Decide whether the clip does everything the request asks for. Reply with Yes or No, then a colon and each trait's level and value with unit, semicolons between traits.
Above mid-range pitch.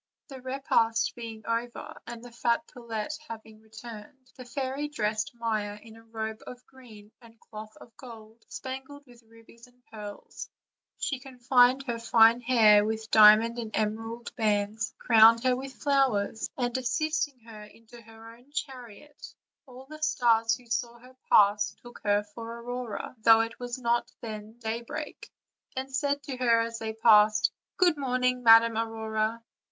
Yes: high, 230 Hz